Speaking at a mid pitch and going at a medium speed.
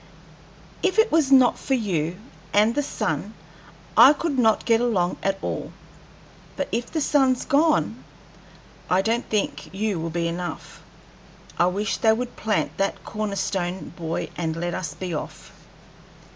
No: high, 210 Hz; average, 155 wpm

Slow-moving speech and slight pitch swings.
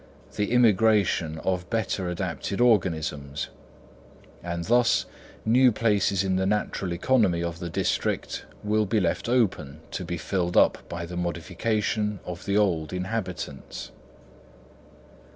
No: slow, 125 wpm; average, 4.0 semitones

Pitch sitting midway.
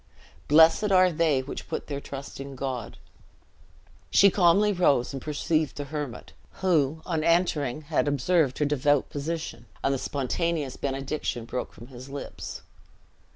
Yes: medium, 145 Hz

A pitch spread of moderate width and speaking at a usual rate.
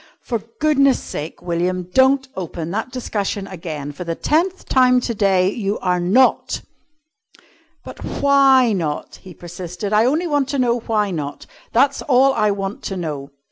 No: wide, 6.7 semitones; average, 160 wpm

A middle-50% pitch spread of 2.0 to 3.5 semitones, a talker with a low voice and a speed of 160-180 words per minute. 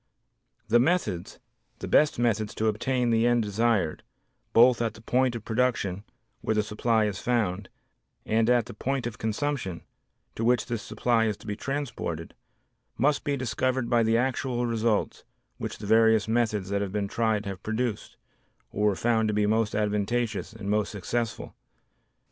Yes: narrow, 2.5 semitones; low, 110 Hz; average, 165 wpm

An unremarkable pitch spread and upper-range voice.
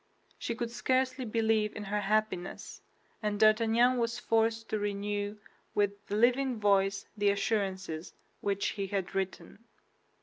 No: narrow, 2.2 semitones; high, 210 Hz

